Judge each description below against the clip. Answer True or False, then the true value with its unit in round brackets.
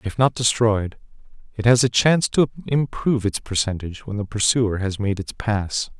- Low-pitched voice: True (110 Hz)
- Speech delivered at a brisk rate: False (180 wpm)